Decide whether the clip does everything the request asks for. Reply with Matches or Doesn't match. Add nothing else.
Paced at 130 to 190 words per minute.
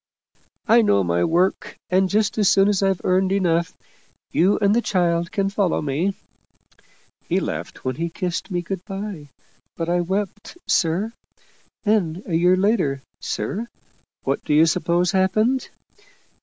Matches